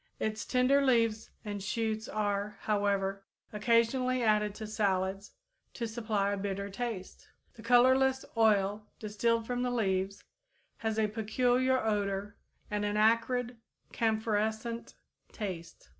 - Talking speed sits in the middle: No, slow, 120 wpm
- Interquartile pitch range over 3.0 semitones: No, narrow, 2.4 semitones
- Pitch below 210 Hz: No, high, 215 Hz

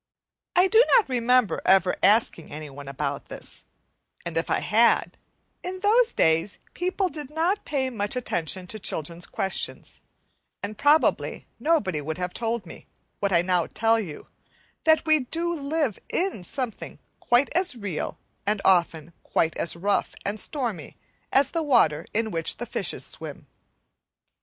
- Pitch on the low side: No, high, 220 Hz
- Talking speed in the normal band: Yes, average, 150 wpm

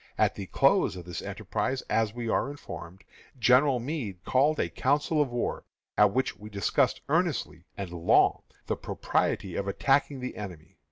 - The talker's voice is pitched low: Yes, low, 115 Hz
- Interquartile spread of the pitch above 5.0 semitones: Yes, wide, 5.6 semitones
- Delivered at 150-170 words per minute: Yes, average, 165 wpm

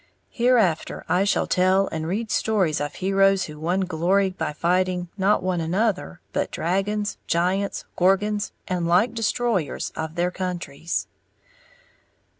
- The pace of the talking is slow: Yes, slow, 130 wpm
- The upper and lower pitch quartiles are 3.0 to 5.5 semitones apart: No, narrow, 2.6 semitones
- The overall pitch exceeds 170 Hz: Yes, medium, 185 Hz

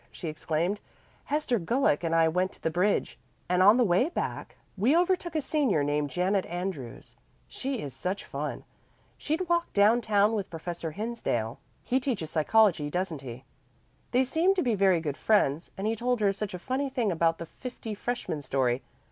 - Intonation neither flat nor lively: No, wide, 7.1 semitones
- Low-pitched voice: No, high, 195 Hz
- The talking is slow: No, average, 180 wpm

